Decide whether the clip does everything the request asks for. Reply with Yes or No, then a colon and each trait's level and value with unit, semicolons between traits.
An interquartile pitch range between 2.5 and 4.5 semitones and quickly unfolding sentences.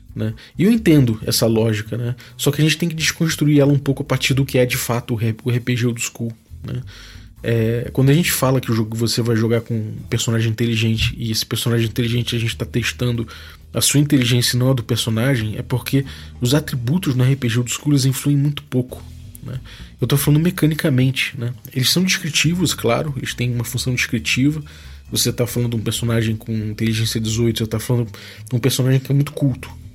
Yes: average, 2.9 semitones; fast, 215 wpm